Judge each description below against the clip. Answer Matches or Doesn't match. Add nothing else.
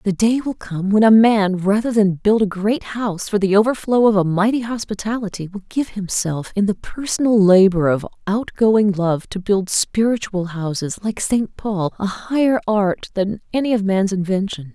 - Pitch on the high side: Matches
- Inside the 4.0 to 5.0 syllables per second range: Matches